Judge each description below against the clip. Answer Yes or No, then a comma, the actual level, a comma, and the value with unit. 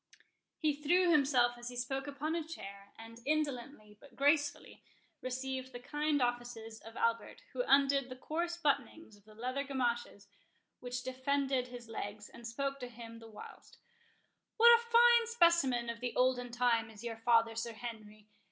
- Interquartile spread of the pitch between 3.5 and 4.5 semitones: Yes, average, 3.8 semitones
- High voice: Yes, very high, 250 Hz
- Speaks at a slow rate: No, average, 160 wpm